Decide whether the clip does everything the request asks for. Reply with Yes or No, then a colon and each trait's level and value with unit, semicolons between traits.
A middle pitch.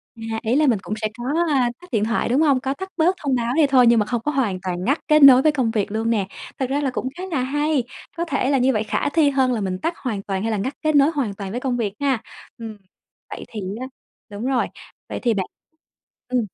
No: very high, 250 Hz